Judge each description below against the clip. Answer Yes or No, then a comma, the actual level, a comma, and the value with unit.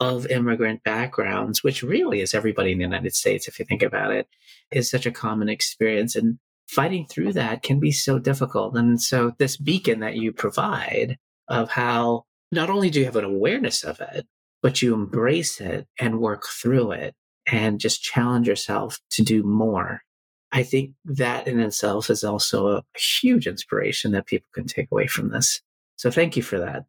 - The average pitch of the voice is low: Yes, low, 120 Hz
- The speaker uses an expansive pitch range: No, average, 3.5 semitones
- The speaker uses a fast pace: No, average, 185 wpm